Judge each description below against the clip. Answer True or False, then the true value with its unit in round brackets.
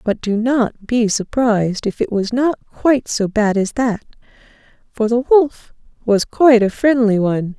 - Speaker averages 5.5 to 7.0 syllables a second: False (4.6 syllables/s)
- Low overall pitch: False (230 Hz)